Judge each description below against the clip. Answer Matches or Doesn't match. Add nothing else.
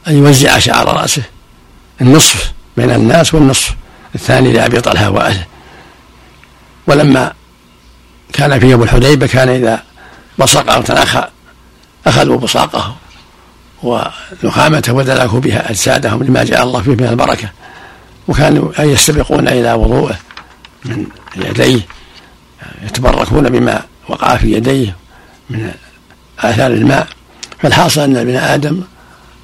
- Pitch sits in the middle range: Doesn't match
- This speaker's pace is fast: Doesn't match